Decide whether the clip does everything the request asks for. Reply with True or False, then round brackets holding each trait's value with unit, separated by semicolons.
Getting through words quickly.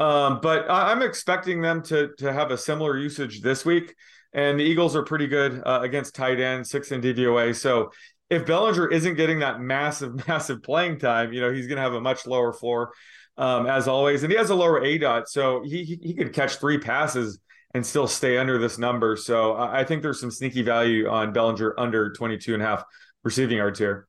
True (215 wpm)